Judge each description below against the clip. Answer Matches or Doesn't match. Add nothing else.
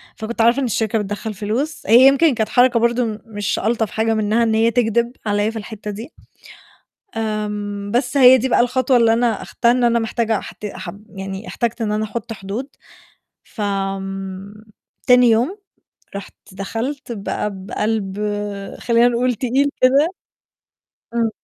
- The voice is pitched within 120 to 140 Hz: Doesn't match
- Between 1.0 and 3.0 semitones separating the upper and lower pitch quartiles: Matches